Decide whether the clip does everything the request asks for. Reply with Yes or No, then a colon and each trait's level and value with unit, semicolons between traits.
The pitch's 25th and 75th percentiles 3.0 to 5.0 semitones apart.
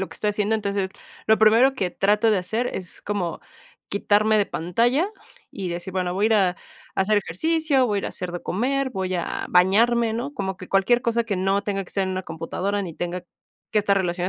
Yes: average, 3.3 semitones